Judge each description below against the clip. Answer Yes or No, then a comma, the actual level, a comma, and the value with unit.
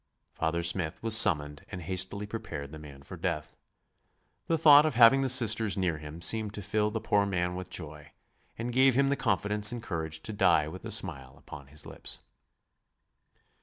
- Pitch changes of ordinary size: No, wide, 6.0 semitones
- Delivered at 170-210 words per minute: Yes, average, 185 wpm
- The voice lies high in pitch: No, very low, 95 Hz